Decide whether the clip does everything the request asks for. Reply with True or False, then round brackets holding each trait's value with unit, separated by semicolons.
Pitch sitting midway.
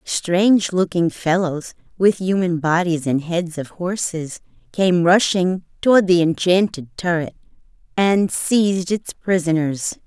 True (180 Hz)